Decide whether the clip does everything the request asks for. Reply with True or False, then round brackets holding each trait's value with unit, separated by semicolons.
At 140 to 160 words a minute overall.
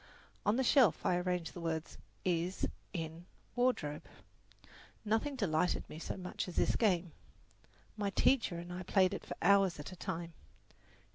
True (155 wpm)